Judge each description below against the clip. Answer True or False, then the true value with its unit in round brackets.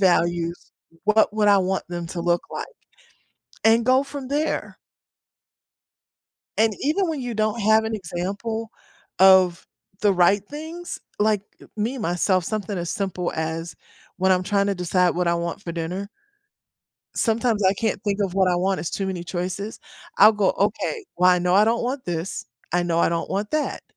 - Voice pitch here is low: False (195 Hz)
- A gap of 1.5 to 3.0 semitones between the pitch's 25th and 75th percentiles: False (3.8 semitones)